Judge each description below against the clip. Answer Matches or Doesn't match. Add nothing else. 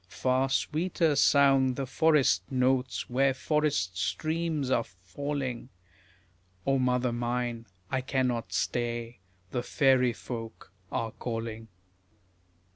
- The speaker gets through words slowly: Matches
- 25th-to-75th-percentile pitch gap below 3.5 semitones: Matches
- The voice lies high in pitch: Doesn't match